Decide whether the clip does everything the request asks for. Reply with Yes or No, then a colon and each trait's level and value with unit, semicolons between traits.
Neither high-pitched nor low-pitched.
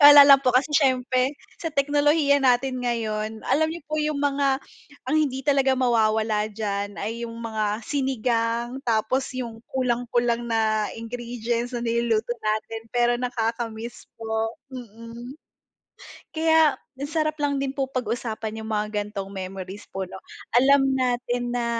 No: high, 240 Hz